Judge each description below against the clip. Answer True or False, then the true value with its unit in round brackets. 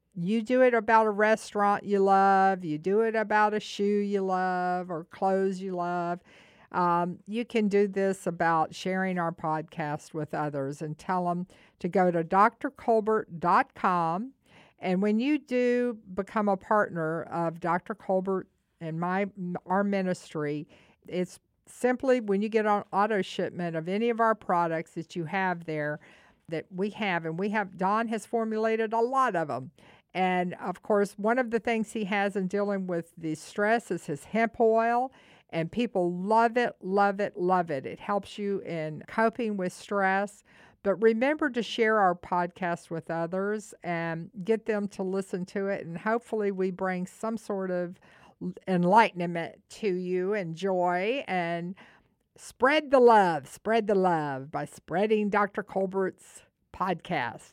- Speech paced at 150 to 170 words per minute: True (160 wpm)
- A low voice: False (195 Hz)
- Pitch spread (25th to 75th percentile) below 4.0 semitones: True (3.6 semitones)